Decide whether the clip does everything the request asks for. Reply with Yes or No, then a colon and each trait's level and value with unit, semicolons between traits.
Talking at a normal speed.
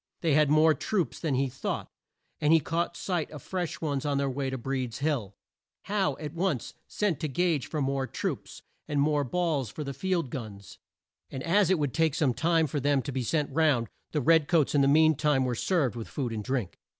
No: fast, 220 wpm